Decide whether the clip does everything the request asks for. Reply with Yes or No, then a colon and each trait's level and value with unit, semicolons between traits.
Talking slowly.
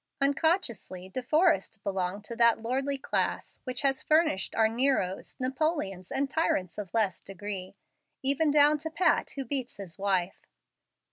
No: average, 145 wpm